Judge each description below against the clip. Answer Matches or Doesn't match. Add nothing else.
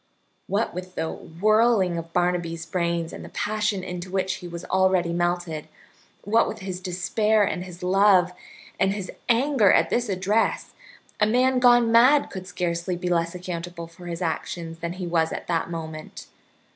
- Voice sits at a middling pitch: Matches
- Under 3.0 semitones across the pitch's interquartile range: Doesn't match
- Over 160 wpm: Matches